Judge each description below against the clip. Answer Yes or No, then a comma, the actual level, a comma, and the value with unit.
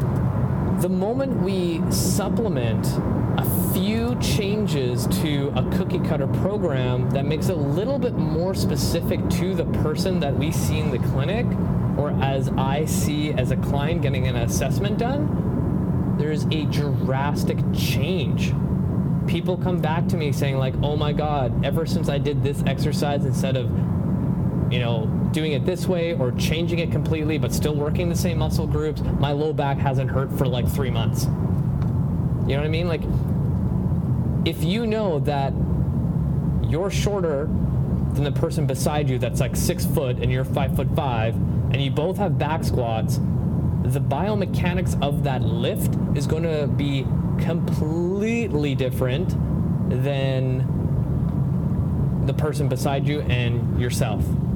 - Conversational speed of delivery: Yes, average, 150 wpm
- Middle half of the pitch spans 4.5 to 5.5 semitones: No, average, 3.2 semitones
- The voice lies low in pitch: No, medium, 150 Hz